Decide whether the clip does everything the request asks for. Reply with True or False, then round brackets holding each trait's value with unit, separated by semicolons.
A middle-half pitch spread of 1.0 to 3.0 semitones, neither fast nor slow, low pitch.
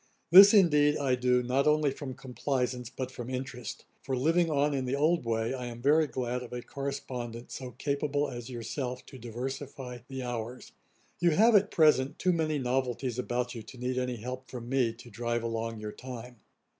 True (2.5 semitones; 190 wpm; 130 Hz)